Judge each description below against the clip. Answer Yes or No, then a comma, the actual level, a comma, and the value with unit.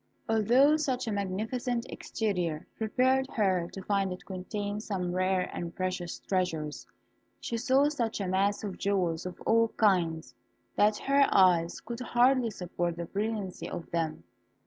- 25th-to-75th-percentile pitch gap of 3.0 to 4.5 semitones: Yes, average, 4.2 semitones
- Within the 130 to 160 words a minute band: Yes, average, 145 wpm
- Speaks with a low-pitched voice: No, high, 200 Hz